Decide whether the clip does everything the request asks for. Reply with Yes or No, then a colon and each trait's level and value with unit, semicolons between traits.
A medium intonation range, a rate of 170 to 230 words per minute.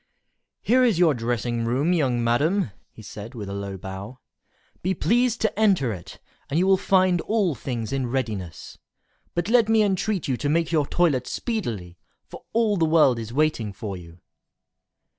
No: wide, 8.7 semitones; average, 175 wpm